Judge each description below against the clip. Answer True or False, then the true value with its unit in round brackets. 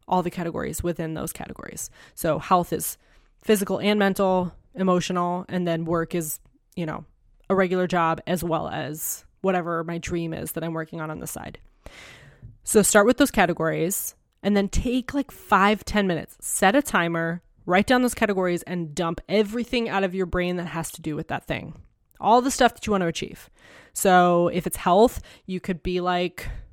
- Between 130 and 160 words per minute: False (190 wpm)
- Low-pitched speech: False (180 Hz)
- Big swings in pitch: False (3.1 semitones)